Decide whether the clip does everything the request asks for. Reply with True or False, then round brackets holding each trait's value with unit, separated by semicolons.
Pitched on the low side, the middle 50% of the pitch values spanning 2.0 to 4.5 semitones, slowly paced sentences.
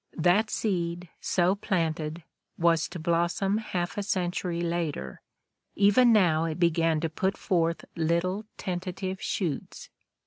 False (175 Hz; 2.4 semitones; 125 wpm)